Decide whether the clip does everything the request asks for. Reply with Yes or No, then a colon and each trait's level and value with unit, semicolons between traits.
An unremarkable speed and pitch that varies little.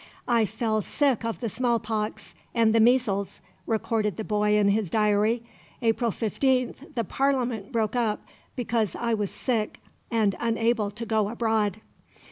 Yes: average, 145 wpm; narrow, 2.0 semitones